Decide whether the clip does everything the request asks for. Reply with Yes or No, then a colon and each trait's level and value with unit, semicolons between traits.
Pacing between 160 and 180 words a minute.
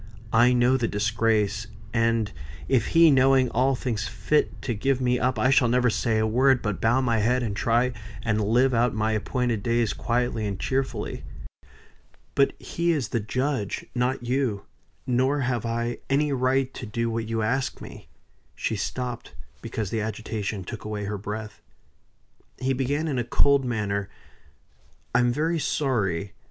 Yes: average, 165 wpm